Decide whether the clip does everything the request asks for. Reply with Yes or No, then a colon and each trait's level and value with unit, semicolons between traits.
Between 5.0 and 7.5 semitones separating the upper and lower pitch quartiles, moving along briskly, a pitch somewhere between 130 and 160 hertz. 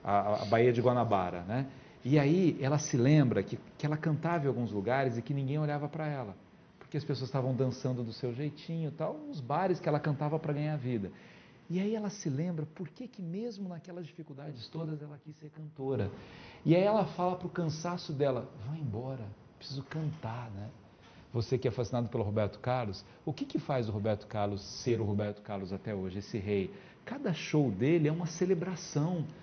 Yes: wide, 5.4 semitones; fast, 200 wpm; medium, 140 Hz